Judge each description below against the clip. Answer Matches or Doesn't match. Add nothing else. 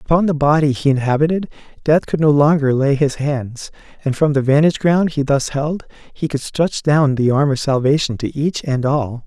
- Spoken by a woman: Doesn't match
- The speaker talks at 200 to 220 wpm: Matches